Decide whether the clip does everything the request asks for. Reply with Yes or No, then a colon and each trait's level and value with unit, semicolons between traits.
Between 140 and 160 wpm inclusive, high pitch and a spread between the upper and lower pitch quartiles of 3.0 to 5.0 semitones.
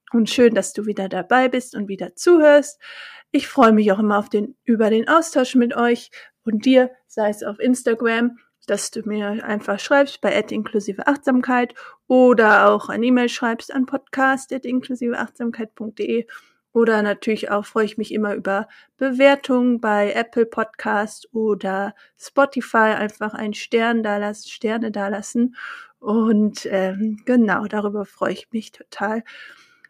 Yes: average, 145 wpm; high, 225 Hz; average, 3.3 semitones